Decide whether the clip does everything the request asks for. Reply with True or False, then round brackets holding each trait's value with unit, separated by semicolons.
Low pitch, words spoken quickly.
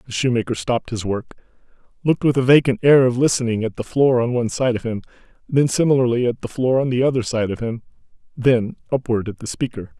True (120 Hz; 215 wpm)